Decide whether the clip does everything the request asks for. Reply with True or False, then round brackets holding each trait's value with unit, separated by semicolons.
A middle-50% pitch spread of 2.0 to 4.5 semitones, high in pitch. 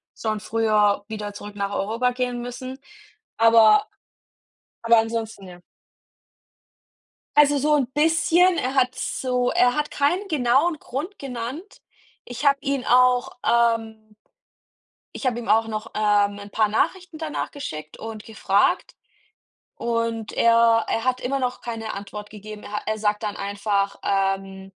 True (3.6 semitones; 230 Hz)